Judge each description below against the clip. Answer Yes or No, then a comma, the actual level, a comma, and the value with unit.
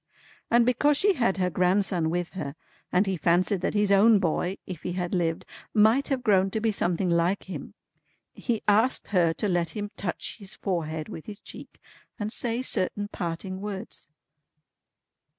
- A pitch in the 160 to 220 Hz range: Yes, high, 190 Hz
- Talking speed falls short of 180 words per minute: Yes, average, 170 wpm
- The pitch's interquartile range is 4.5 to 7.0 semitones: No, average, 3.3 semitones